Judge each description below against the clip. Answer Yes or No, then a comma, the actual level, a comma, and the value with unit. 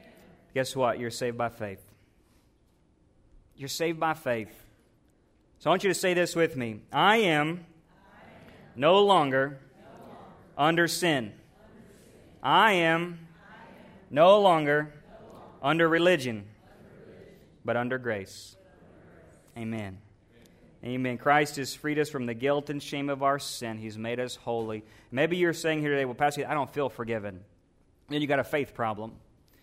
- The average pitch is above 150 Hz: No, low, 135 Hz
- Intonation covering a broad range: Yes, wide, 6.3 semitones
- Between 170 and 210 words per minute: No, average, 145 wpm